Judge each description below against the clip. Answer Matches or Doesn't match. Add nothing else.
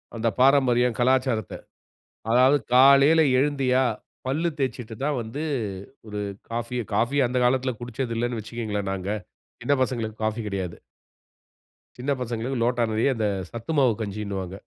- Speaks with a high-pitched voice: Doesn't match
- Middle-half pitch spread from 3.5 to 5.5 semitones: Doesn't match